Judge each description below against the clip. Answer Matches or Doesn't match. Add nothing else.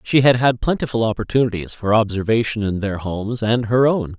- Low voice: Matches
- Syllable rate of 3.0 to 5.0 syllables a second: Doesn't match